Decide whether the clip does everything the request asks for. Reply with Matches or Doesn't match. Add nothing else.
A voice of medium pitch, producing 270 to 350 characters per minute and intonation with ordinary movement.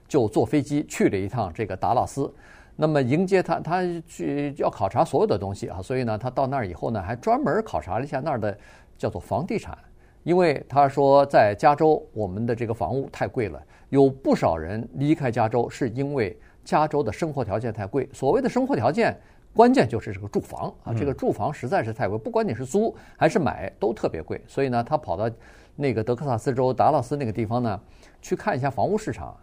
Doesn't match